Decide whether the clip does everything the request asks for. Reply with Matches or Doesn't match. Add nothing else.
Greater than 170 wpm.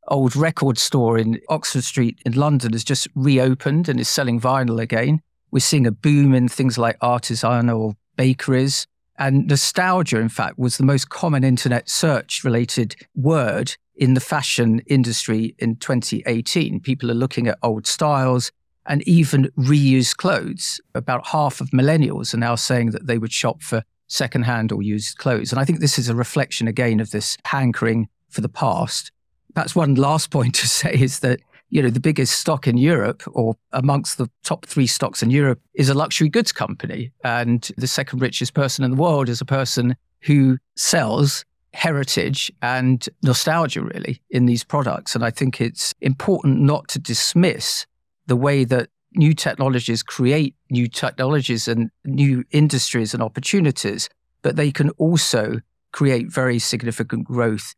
Doesn't match